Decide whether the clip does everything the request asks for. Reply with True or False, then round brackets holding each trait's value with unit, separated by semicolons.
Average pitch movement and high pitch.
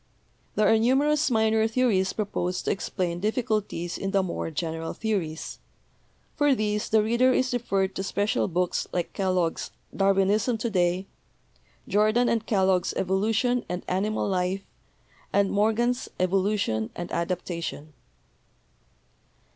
True (3.4 semitones; 200 Hz)